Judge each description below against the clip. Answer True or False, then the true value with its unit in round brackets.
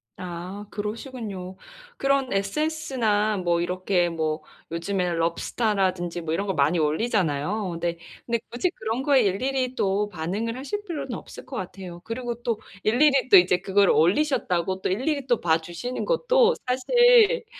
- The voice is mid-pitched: False (205 Hz)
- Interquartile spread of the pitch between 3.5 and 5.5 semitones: False (6.5 semitones)